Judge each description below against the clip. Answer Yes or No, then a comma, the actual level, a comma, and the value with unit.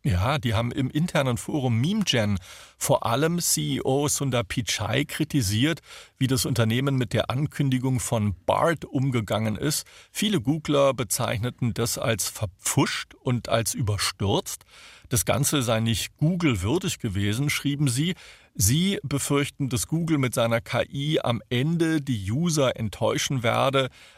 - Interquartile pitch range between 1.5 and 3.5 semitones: No, average, 4.2 semitones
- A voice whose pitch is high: No, low, 130 Hz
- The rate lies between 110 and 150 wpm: Yes, average, 130 wpm